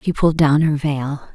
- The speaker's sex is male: No, female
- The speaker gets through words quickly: Yes, fast, 225 wpm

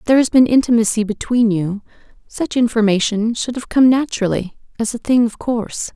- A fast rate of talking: No, average, 170 wpm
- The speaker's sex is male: No, female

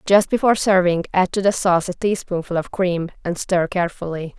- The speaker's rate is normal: Yes, average, 190 wpm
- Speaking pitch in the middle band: Yes, medium, 180 Hz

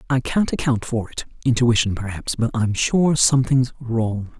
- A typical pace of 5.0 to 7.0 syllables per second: No, 4.6 syllables/s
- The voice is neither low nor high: No, low, 120 Hz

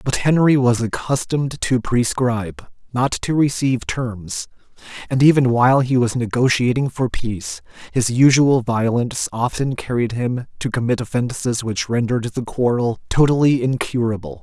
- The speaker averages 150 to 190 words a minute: No, slow, 135 wpm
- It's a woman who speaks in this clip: No, male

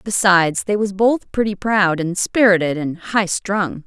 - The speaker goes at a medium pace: Yes, average, 170 wpm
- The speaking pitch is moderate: No, high, 195 Hz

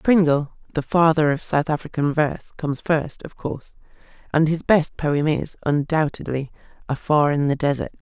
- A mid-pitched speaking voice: Yes, medium, 150 Hz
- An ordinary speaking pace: Yes, average, 155 wpm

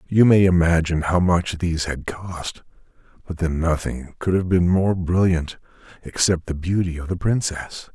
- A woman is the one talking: No, male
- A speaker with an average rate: Yes, average, 165 wpm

